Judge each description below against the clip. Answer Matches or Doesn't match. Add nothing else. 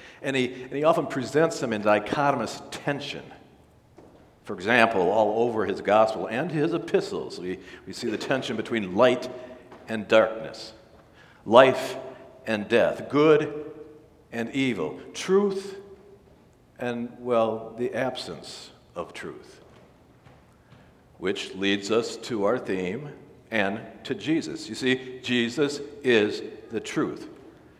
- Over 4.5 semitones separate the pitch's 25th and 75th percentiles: Matches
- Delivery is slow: Matches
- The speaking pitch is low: Matches